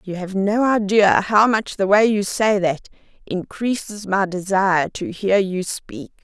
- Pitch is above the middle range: Yes, high, 195 Hz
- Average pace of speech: Yes, average, 175 wpm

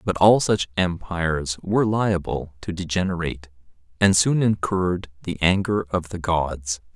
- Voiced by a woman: No, male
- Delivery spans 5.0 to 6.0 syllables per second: No, 4.5 syllables/s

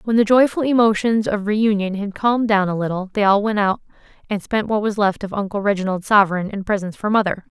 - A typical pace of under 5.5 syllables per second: No, 6.0 syllables/s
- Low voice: No, high, 205 Hz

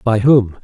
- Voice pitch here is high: No, low, 115 Hz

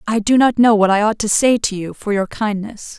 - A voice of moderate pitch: No, high, 215 Hz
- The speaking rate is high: Yes, fast, 280 wpm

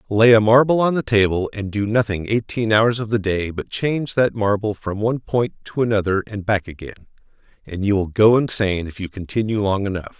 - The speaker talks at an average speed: No, fast, 210 wpm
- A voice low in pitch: Yes, low, 105 Hz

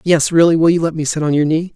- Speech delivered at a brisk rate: Yes, fast, 340 wpm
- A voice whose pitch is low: No, medium, 160 Hz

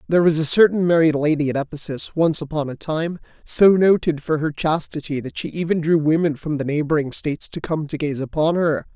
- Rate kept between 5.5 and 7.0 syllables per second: Yes, 5.7 syllables/s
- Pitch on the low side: No, medium, 155 Hz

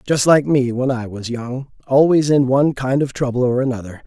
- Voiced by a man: Yes, male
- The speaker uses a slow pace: No, fast, 205 wpm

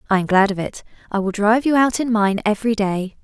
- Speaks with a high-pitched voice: Yes, high, 210 Hz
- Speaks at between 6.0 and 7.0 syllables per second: Yes, 6.3 syllables/s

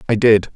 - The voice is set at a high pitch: No, low, 110 Hz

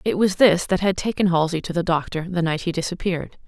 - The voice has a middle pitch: Yes, medium, 175 Hz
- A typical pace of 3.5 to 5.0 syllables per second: No, 6.1 syllables/s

